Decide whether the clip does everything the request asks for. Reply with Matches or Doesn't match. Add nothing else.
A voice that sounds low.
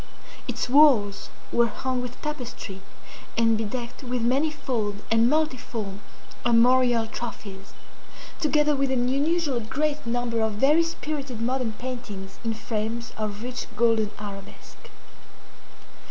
Doesn't match